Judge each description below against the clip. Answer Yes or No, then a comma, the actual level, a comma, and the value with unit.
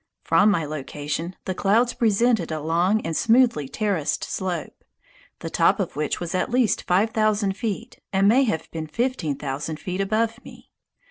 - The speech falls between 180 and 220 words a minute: No, average, 165 wpm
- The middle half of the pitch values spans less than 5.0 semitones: No, wide, 5.6 semitones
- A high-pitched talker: Yes, high, 195 Hz